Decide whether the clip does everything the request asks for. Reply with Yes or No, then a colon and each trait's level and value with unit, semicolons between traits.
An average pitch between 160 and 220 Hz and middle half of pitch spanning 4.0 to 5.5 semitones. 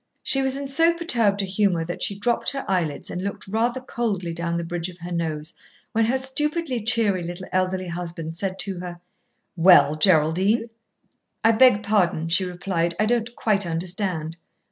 Yes: high, 190 Hz; average, 4.9 semitones